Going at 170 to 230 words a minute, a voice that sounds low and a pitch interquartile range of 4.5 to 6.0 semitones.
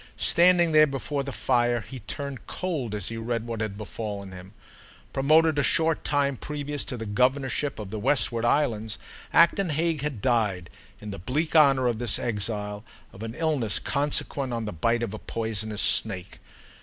Yes: average, 175 wpm; low, 120 Hz; average, 5.1 semitones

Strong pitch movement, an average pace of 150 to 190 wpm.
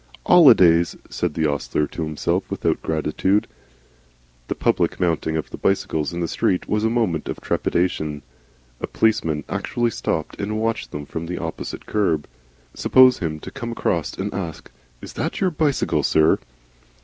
Yes: wide, 5.9 semitones; average, 160 wpm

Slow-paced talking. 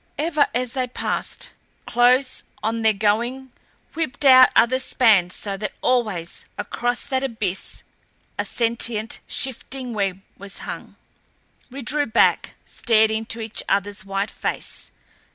Yes: slow, 130 wpm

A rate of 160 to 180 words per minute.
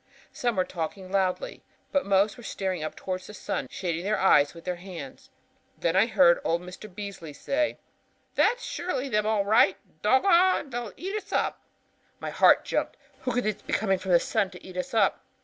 No: average, 190 wpm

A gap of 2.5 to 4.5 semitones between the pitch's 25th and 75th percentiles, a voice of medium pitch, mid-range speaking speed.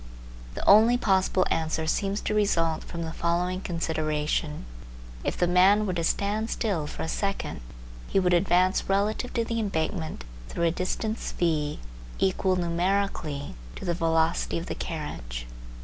Yes: average, 3.5 semitones; medium, 175 Hz; average, 150 wpm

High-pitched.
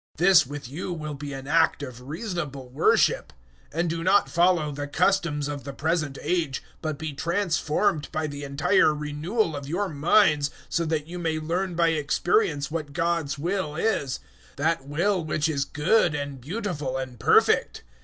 No: medium, 155 Hz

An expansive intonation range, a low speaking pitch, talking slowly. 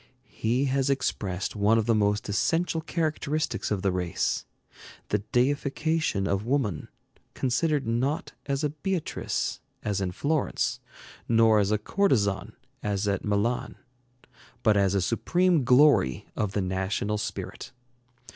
Yes: wide, 6.1 semitones; low, 115 Hz; slow, 130 wpm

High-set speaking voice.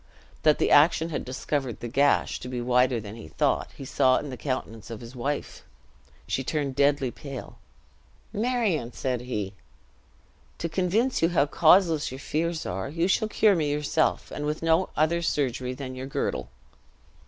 No: medium, 145 Hz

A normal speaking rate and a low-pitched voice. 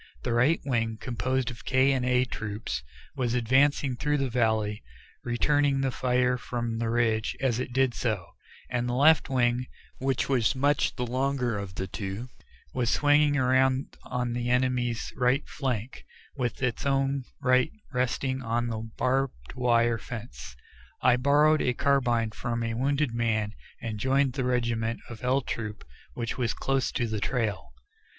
Yes: average, 160 wpm; low, 125 Hz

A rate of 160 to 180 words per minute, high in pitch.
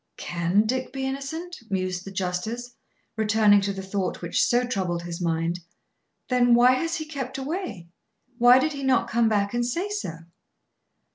Yes: average, 165 wpm; high, 235 Hz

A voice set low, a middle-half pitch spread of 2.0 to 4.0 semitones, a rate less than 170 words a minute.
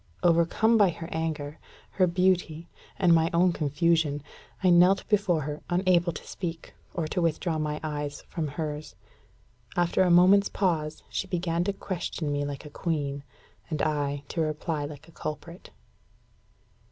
No: medium, 165 Hz; average, 2.8 semitones; average, 155 wpm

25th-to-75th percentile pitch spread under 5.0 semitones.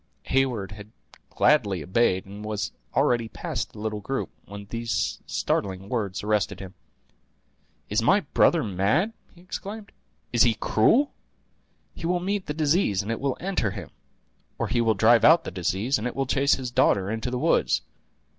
No: wide, 5.5 semitones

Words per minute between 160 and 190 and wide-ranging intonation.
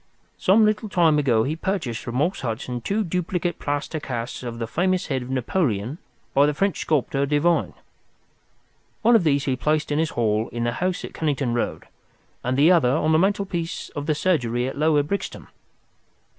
Yes: average, 185 wpm; wide, 5.9 semitones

